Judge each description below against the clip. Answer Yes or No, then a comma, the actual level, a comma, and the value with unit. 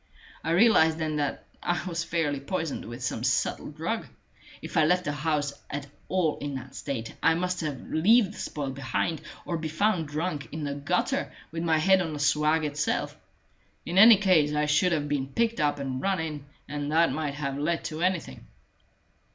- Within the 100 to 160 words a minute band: No, average, 190 wpm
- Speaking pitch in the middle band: Yes, medium, 155 Hz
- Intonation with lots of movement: No, average, 2.9 semitones